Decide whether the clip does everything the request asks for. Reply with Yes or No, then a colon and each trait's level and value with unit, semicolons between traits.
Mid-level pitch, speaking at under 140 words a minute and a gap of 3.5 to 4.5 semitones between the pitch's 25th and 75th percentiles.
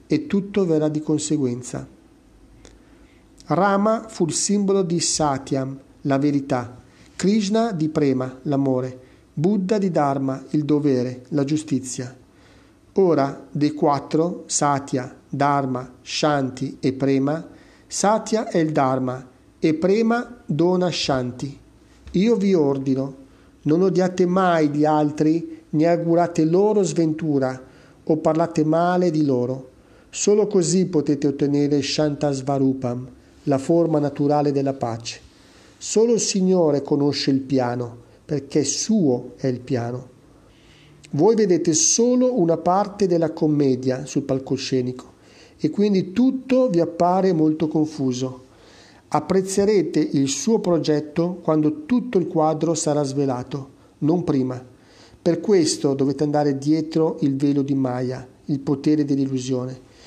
Yes: medium, 150 Hz; average, 120 wpm; average, 4.2 semitones